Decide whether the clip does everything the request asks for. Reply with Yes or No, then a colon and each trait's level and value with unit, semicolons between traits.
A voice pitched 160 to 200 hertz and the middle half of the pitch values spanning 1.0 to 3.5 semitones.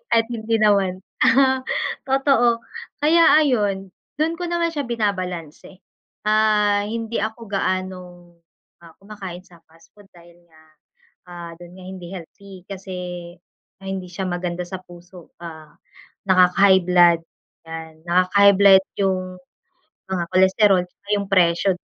Yes: high, 190 Hz; average, 3.2 semitones